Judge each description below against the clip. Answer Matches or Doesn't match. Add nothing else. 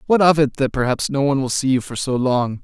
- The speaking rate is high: Matches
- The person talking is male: Matches